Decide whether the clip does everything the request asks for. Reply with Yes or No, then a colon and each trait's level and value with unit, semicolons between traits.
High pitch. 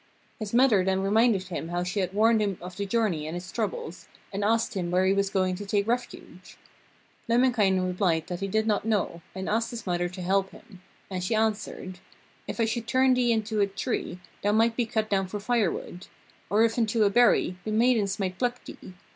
Yes: high, 205 Hz